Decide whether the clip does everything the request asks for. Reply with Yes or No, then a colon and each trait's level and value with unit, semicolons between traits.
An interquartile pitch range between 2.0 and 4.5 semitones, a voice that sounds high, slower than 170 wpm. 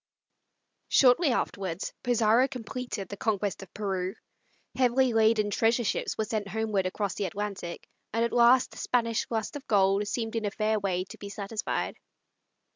Yes: average, 2.8 semitones; high, 215 Hz; average, 160 wpm